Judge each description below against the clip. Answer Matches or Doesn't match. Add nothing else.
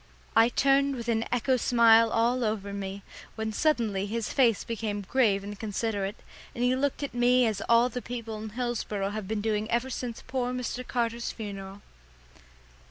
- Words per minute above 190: Doesn't match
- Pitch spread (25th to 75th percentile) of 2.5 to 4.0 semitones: Matches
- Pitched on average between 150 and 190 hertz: Doesn't match